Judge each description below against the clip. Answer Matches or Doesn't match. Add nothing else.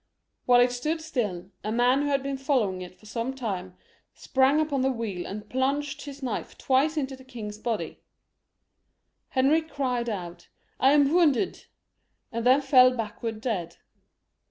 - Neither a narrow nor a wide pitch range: Matches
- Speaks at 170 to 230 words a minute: Matches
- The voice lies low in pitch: Doesn't match